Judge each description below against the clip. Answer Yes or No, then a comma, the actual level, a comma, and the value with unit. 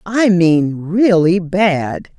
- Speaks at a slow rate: Yes, slow, 110 wpm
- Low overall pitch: No, medium, 180 Hz